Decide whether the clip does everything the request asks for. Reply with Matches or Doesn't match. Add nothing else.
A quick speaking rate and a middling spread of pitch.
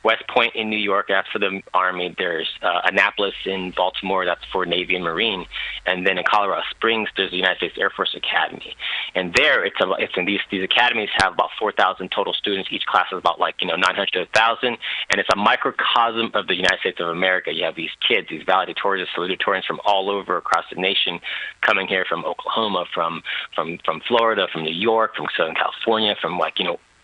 Doesn't match